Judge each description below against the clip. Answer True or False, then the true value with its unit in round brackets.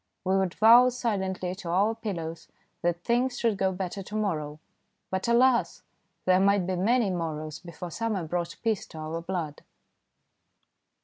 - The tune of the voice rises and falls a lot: False (4.4 semitones)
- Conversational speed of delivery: True (150 wpm)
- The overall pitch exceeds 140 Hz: True (190 Hz)